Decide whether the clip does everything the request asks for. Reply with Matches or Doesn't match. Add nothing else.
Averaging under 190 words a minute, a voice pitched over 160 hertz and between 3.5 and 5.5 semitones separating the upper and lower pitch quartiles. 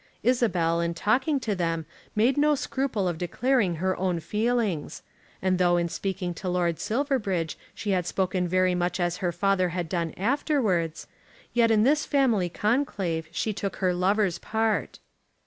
Matches